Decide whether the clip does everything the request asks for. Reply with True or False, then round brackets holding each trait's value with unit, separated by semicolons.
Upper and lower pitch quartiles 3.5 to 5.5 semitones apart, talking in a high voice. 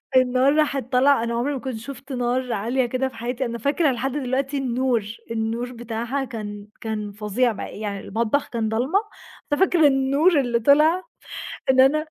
False (3.1 semitones; 255 Hz)